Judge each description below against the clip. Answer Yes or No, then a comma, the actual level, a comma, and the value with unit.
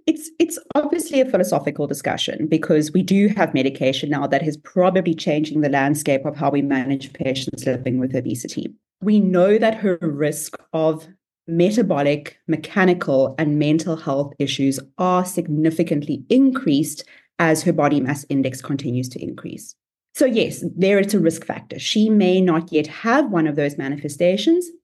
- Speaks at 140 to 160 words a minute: Yes, average, 155 wpm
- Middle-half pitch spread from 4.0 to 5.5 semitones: Yes, average, 4.8 semitones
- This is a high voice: No, medium, 160 Hz